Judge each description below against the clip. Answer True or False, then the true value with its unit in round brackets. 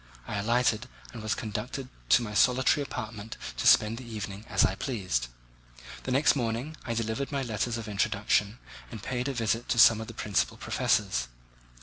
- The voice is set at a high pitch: False (115 Hz)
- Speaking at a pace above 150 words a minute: True (180 wpm)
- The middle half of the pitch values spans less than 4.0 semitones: True (2.9 semitones)